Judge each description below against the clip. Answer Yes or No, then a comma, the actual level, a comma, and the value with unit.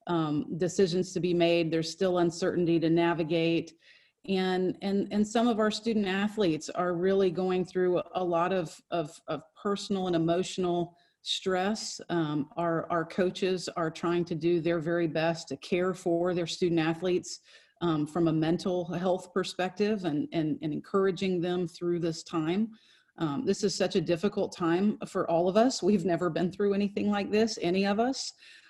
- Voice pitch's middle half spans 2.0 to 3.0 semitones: Yes, narrow, 2.5 semitones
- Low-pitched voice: No, medium, 180 Hz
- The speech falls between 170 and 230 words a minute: Yes, average, 175 wpm